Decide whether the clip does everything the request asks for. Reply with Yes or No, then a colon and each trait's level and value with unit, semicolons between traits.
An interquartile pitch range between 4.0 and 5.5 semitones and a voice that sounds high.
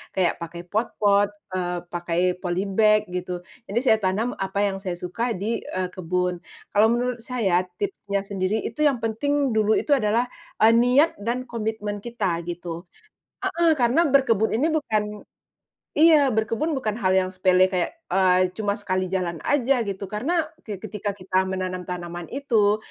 Yes: average, 4.4 semitones; high, 205 Hz